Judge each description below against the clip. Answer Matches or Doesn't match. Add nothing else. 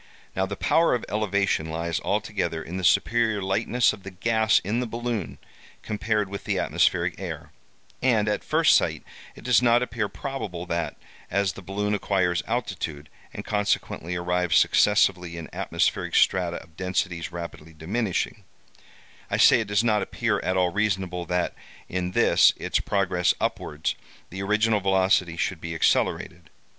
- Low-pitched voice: Matches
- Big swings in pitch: Doesn't match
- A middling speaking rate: Matches